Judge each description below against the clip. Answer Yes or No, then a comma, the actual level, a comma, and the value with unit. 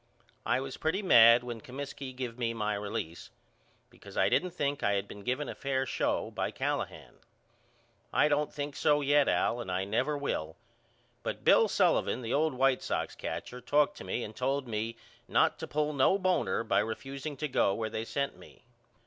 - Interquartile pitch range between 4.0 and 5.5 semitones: Yes, average, 4.3 semitones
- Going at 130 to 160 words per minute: No, average, 190 wpm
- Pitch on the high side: No, low, 130 Hz